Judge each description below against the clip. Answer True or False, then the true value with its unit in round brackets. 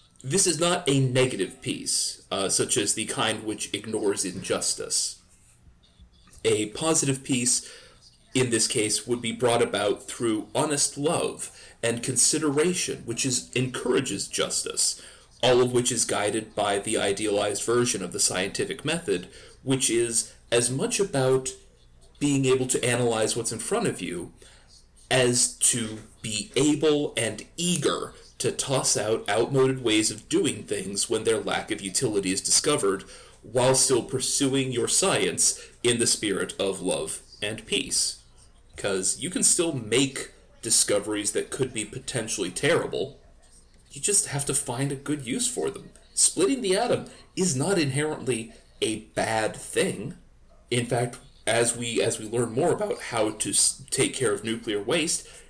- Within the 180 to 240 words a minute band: False (150 wpm)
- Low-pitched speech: True (125 Hz)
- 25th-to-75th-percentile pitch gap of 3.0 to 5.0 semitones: True (4.1 semitones)